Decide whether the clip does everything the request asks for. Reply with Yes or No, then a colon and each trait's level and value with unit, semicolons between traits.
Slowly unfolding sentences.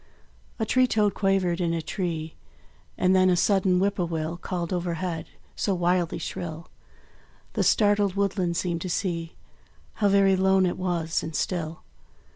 No: average, 155 wpm